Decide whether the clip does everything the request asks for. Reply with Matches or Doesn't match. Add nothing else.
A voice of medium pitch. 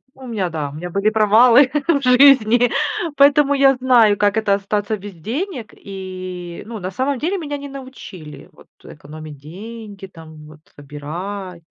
Doesn't match